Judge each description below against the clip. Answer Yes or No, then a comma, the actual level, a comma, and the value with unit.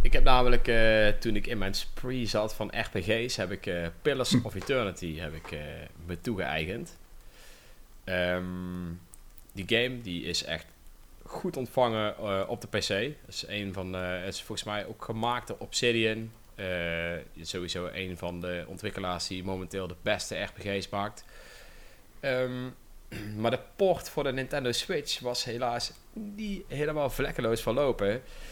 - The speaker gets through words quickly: No, average, 145 wpm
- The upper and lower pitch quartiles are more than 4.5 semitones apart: Yes, average, 5.0 semitones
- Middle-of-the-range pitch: No, low, 105 Hz